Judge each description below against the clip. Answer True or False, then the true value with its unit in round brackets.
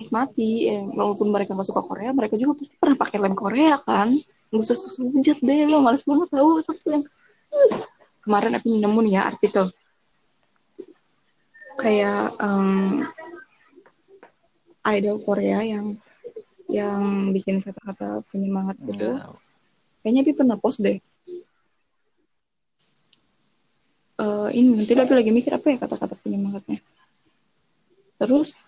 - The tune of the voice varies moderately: False (6.5 semitones)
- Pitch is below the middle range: False (235 Hz)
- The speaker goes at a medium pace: True (120 wpm)